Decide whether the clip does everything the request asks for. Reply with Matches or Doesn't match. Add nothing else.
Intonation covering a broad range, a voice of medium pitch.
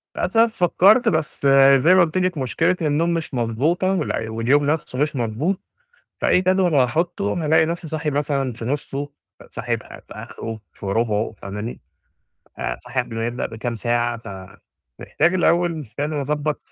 Matches